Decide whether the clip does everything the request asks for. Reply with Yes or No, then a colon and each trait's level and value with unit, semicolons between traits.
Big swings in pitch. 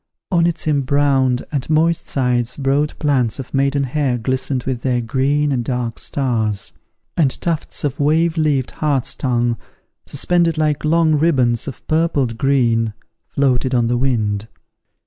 No: average, 3.5 semitones